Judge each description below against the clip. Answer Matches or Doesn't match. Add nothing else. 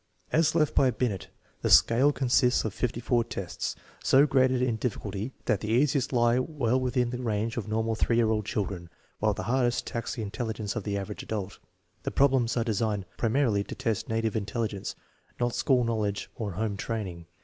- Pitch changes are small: Doesn't match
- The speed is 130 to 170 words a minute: Doesn't match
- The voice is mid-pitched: Doesn't match